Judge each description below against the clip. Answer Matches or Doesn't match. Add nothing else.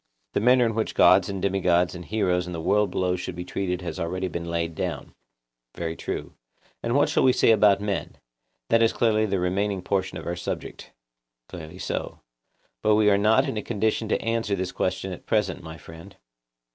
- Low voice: Matches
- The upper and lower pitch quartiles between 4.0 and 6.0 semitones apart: Doesn't match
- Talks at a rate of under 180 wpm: Doesn't match